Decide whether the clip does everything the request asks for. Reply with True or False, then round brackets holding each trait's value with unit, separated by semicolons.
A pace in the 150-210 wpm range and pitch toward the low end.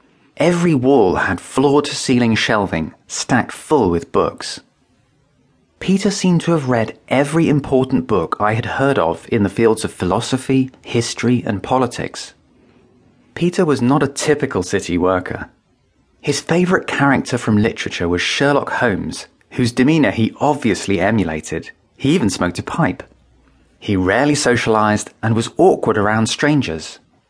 False (140 wpm; 125 Hz)